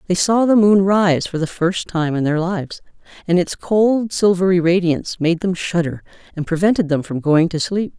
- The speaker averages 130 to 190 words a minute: No, fast, 205 wpm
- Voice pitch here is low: No, medium, 180 Hz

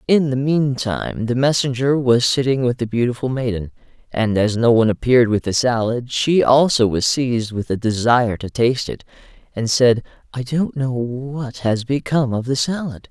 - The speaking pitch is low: Yes, low, 125 Hz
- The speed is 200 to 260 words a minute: No, average, 185 wpm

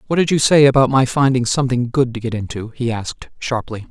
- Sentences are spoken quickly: Yes, fast, 230 wpm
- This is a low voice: Yes, low, 125 Hz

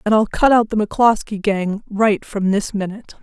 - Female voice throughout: Yes, female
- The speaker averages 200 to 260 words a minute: Yes, fast, 205 wpm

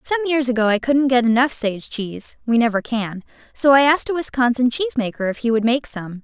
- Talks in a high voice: Yes, high, 245 Hz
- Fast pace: Yes, fast, 220 wpm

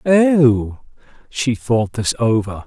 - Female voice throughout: No, male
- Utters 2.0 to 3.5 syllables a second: Yes, 2.9 syllables/s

